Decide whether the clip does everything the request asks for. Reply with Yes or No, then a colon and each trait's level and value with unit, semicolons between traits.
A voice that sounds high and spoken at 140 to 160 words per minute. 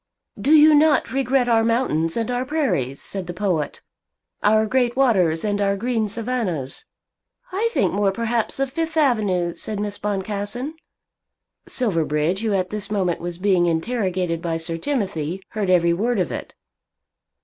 Yes: high, 205 Hz; average, 155 wpm